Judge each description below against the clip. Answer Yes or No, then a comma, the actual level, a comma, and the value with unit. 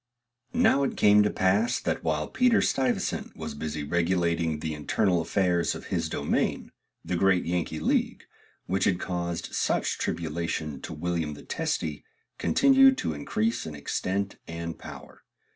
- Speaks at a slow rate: No, average, 145 wpm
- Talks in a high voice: No, very low, 85 Hz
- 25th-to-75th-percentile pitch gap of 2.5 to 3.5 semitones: No, average, 3.9 semitones